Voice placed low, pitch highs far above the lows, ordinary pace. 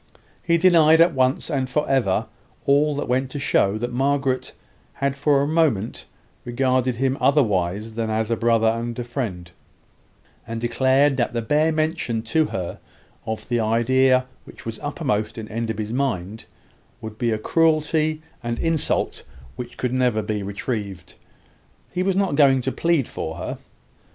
No: low, 130 Hz; average, 4.5 semitones; average, 160 wpm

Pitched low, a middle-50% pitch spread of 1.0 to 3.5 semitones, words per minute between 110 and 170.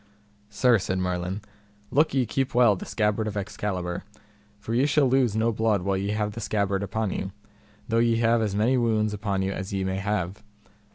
No: low, 105 Hz; average, 2.9 semitones; average, 195 wpm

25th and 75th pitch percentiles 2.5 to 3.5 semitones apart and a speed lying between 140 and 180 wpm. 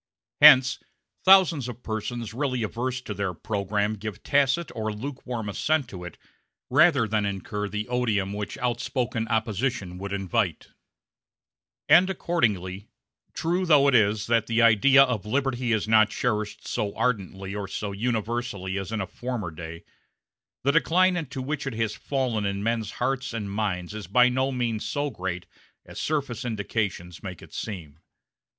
No: average, 4.1 semitones; average, 155 wpm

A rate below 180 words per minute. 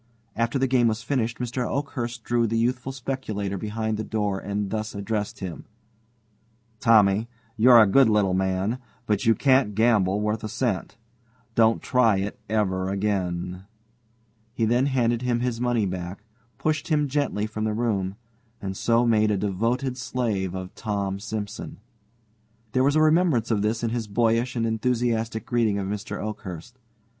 Yes: average, 160 wpm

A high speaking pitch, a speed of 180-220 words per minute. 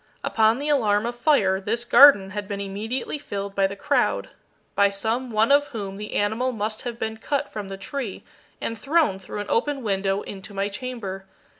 Yes: high, 215 Hz; average, 190 wpm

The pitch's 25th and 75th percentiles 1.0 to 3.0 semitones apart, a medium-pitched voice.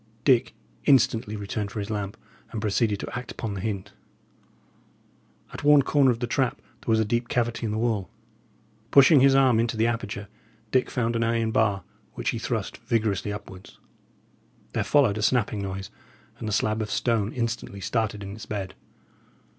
No: narrow, 2.6 semitones; low, 110 Hz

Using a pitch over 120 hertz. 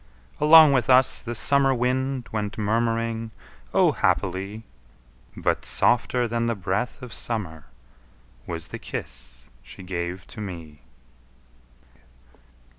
No: low, 115 Hz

